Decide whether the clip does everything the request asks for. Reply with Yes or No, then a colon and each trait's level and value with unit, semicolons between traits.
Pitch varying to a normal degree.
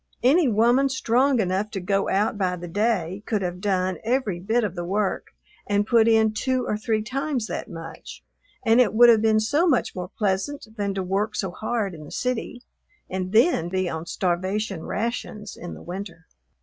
Yes: average, 4.0 semitones